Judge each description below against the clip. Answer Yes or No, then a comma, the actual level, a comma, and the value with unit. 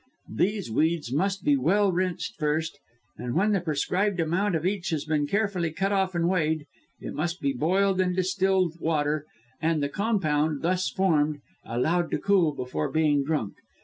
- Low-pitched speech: No, medium, 165 Hz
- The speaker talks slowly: No, average, 175 wpm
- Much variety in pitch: No, average, 4.0 semitones